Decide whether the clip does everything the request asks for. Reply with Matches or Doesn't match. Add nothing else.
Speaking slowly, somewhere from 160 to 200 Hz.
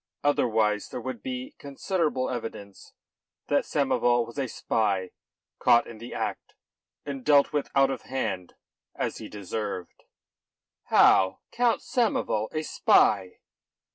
Doesn't match